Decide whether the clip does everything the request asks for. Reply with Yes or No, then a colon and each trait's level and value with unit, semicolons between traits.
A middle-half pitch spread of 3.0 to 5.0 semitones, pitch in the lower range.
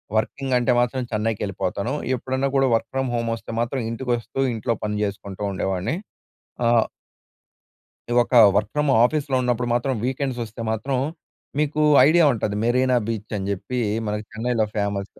Yes: average, 3.6 semitones; low, 120 Hz